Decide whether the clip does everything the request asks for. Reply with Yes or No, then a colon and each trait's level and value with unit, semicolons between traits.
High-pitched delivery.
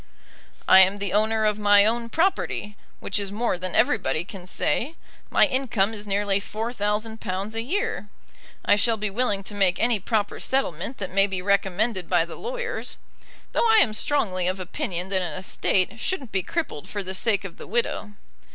Yes: high, 205 Hz